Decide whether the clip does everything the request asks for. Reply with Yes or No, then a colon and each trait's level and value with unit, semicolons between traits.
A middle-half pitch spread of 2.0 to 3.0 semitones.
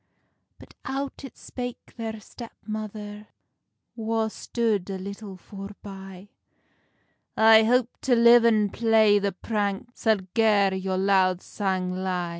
Yes: narrow, 2.6 semitones